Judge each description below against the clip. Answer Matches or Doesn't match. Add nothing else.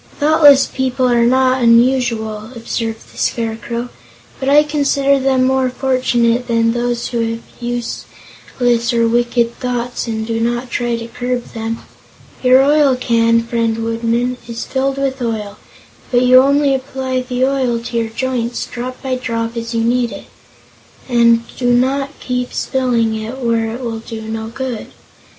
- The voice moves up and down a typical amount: Doesn't match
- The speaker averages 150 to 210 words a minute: Matches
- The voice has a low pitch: Doesn't match